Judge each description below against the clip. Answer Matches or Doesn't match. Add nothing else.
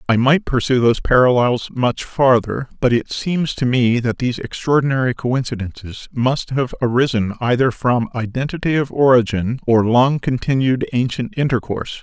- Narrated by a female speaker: Doesn't match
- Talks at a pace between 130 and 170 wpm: Matches